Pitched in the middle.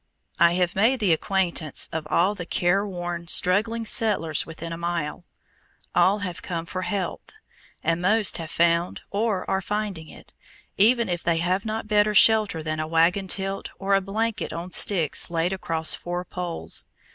Yes: medium, 180 Hz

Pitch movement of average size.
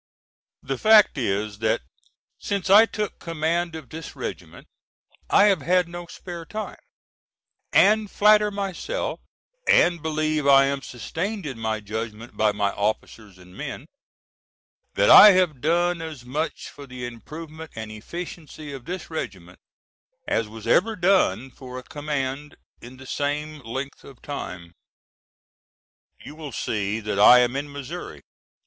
No: wide, 6.7 semitones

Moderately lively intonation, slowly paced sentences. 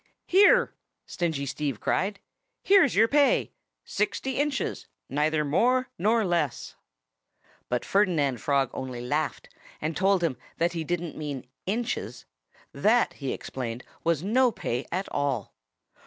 No: wide, 7.6 semitones; slow, 125 wpm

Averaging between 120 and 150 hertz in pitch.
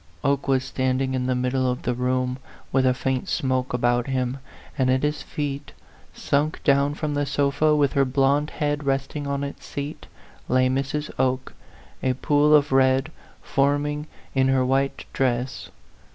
Yes: low, 135 Hz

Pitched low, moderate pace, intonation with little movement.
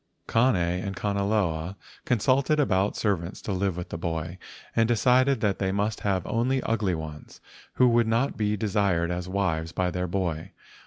No: low, 100 Hz; average, 165 wpm; average, 4.2 semitones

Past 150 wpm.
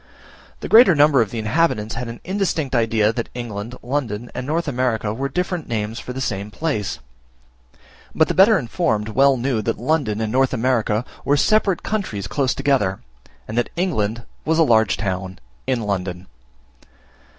Yes: average, 165 wpm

